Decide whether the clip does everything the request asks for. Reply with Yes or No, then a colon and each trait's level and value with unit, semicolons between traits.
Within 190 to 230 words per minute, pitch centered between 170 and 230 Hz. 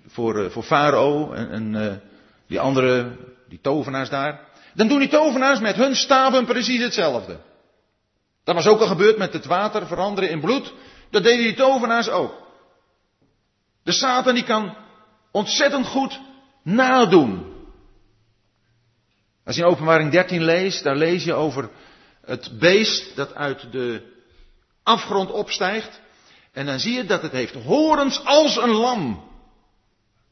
No: average, 140 wpm; high, 190 Hz